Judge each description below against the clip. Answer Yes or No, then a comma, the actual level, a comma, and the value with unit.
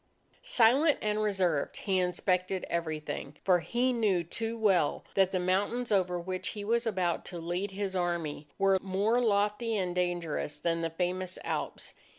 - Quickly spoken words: No, average, 160 wpm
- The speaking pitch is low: No, medium, 185 Hz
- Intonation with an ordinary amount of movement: Yes, average, 3.2 semitones